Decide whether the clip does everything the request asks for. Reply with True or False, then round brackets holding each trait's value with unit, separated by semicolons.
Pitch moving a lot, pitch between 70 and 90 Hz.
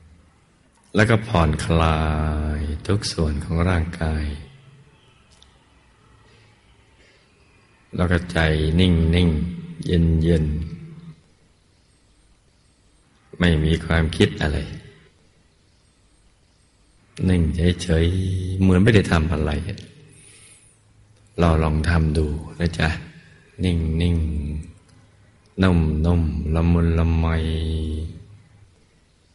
False (3.6 semitones; 85 Hz)